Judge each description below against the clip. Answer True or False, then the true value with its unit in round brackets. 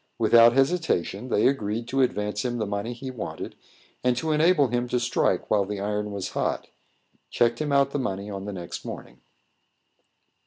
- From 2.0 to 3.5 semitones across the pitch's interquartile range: False (4.2 semitones)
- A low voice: True (120 Hz)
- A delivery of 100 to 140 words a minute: False (180 wpm)